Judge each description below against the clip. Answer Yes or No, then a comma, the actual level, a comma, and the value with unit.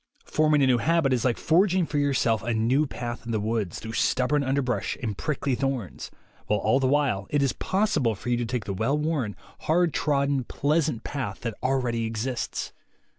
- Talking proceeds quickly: Yes, fast, 225 wpm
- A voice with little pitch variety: No, average, 4.2 semitones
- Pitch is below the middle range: Yes, low, 130 Hz